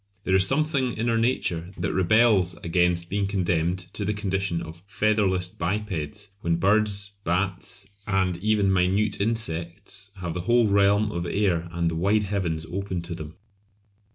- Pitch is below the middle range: Yes, very low, 95 Hz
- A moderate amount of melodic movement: Yes, average, 3.2 semitones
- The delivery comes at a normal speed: Yes, average, 155 wpm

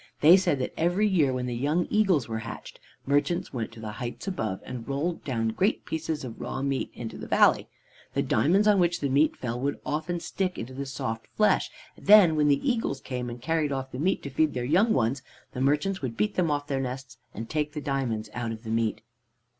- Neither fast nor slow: No, fast, 225 wpm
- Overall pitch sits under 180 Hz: Yes, medium, 140 Hz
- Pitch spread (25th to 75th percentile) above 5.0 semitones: Yes, wide, 5.5 semitones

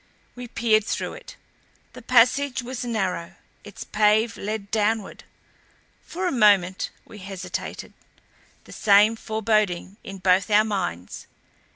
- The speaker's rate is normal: No, slow, 125 wpm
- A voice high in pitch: Yes, high, 210 Hz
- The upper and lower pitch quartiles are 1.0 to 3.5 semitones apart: Yes, narrow, 2.6 semitones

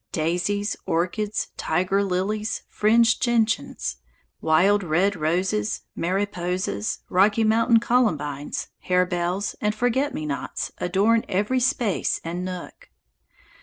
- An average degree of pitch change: Yes, average, 3.6 semitones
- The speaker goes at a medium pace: No, slow, 100 wpm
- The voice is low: No, high, 195 Hz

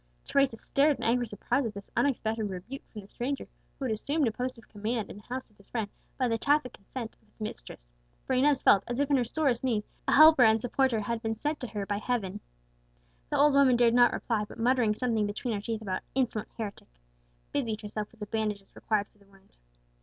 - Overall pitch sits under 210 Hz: No, high, 230 Hz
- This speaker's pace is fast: Yes, fast, 230 wpm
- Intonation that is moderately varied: Yes, average, 3.6 semitones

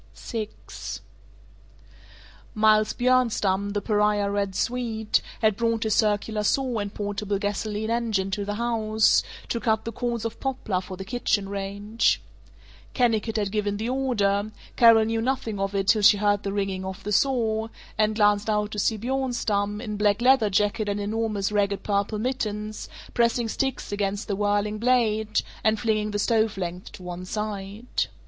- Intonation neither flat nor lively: No, narrow, 1.9 semitones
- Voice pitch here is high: Yes, high, 210 Hz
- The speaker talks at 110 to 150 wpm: No, average, 160 wpm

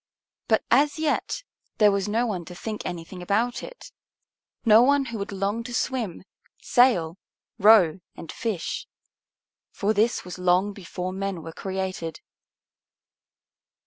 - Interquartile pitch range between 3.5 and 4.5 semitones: Yes, average, 4.1 semitones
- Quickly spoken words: No, slow, 135 wpm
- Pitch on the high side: Yes, high, 200 Hz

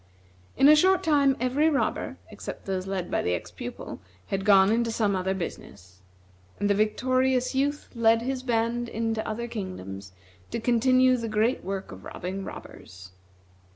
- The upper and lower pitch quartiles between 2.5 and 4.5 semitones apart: No, average, 5.0 semitones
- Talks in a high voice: Yes, high, 225 Hz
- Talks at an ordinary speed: Yes, average, 160 wpm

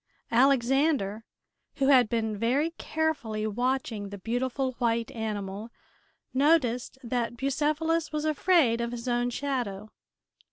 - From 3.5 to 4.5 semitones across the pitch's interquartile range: Yes, average, 3.8 semitones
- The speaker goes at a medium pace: No, slow, 115 wpm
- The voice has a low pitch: No, high, 245 Hz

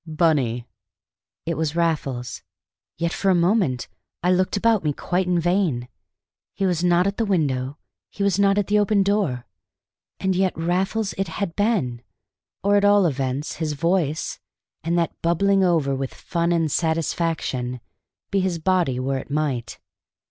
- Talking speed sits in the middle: Yes, average, 160 wpm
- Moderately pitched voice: Yes, medium, 170 Hz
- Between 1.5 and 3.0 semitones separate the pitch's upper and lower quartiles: No, average, 4.9 semitones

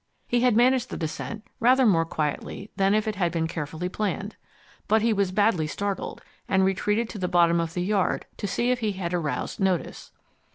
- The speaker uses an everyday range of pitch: Yes, average, 4.1 semitones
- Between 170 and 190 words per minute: No, average, 200 wpm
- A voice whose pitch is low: No, high, 195 Hz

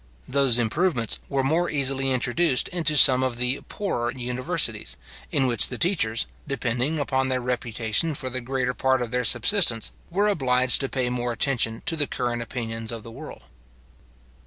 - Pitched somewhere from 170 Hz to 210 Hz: No, low, 130 Hz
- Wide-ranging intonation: No, average, 2.8 semitones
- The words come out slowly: No, average, 165 wpm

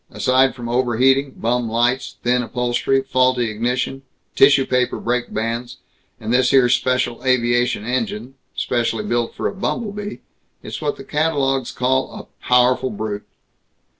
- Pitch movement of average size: No, narrow, 1.8 semitones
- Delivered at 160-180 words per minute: No, average, 140 wpm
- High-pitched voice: No, low, 125 Hz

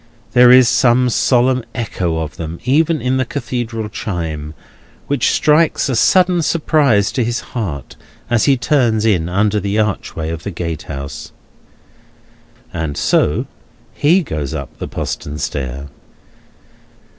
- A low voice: Yes, low, 110 Hz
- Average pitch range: No, wide, 7.9 semitones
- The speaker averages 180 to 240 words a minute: No, slow, 135 wpm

